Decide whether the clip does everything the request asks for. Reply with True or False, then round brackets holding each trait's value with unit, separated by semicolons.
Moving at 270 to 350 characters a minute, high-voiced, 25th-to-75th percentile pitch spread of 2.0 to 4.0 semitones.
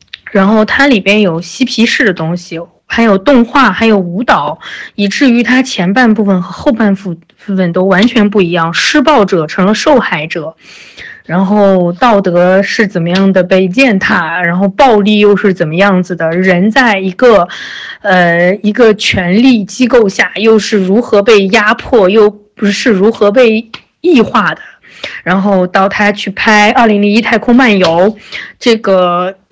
False (235 characters per minute; 205 Hz; 3.4 semitones)